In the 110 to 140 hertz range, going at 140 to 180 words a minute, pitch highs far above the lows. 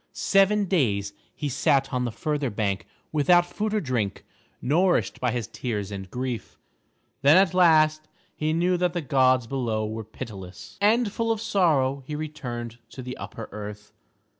Yes: low, 135 Hz; average, 165 wpm; wide, 7.4 semitones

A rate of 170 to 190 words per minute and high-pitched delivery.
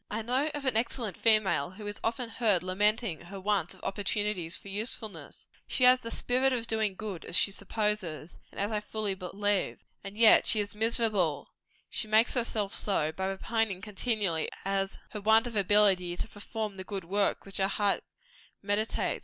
Yes: average, 180 wpm; high, 210 Hz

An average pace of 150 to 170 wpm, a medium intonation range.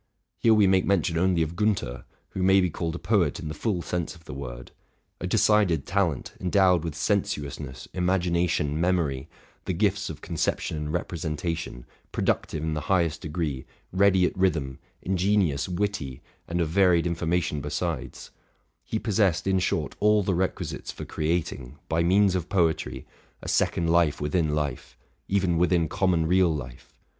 Yes: average, 165 wpm; average, 3.6 semitones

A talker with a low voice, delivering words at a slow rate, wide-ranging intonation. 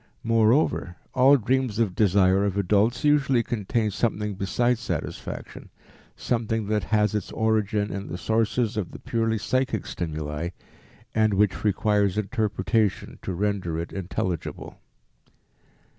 No: low, 105 Hz; slow, 125 wpm; average, 2.8 semitones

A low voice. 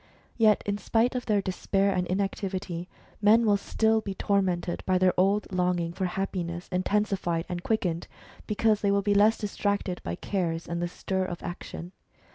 No: high, 195 Hz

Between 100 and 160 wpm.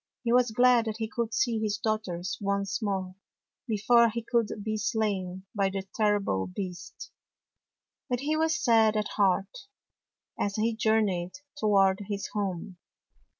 Yes: average, 150 wpm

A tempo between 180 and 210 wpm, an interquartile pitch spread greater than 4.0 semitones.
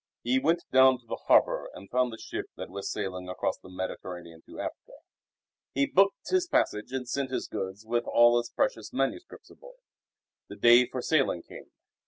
Yes: average, 185 wpm; wide, 5.6 semitones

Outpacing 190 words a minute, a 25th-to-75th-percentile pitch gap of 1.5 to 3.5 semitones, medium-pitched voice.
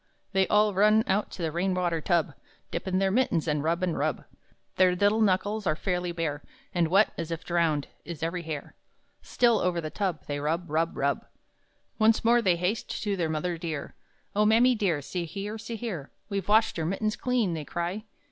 No: average, 200 wpm; average, 4.2 semitones; medium, 180 Hz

